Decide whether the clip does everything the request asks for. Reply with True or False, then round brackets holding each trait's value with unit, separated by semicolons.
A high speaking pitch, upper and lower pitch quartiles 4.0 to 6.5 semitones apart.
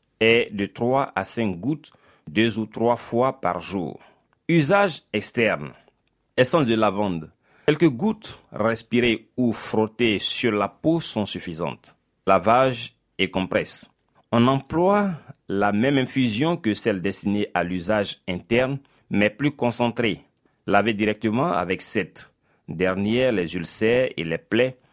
False (115 Hz; 4.5 semitones)